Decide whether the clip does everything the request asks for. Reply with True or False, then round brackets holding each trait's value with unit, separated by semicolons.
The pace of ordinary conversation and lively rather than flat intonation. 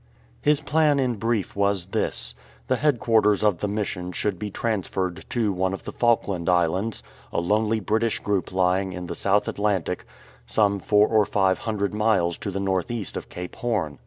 False (180 wpm; 3.1 semitones)